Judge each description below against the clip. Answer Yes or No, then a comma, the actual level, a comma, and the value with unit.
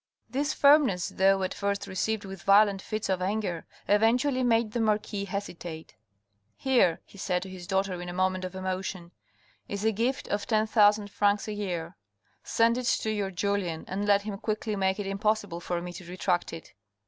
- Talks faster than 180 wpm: Yes, average, 195 wpm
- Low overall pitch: No, high, 200 Hz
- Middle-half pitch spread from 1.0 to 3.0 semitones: Yes, narrow, 2.6 semitones